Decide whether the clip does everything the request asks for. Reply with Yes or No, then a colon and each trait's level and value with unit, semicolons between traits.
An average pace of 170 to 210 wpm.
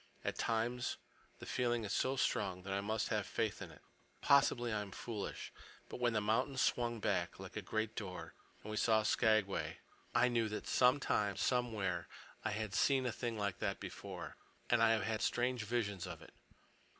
Yes: average, 180 wpm